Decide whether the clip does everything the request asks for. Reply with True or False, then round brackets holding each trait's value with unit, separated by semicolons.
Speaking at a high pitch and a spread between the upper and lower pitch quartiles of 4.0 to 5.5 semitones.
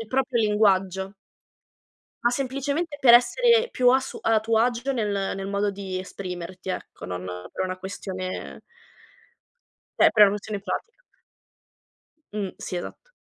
True (210 Hz; 4.7 semitones)